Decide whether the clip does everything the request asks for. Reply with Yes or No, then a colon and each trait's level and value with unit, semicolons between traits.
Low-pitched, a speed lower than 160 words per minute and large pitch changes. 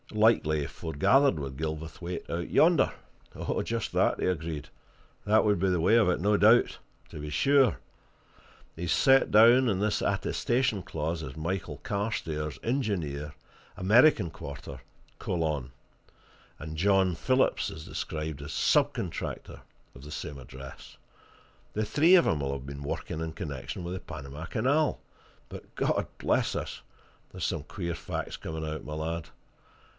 Yes: very low, 85 Hz; average, 150 wpm; wide, 6.0 semitones